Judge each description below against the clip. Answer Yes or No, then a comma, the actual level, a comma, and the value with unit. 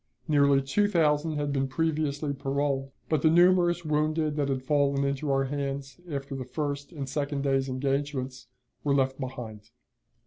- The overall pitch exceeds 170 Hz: No, medium, 140 Hz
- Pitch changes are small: Yes, narrow, 1.9 semitones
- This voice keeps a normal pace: Yes, average, 160 wpm